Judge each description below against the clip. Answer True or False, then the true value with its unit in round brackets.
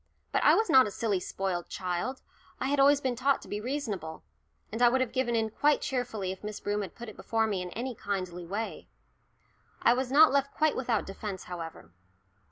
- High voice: True (225 Hz)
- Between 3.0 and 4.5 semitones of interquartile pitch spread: False (5.2 semitones)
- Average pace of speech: False (210 wpm)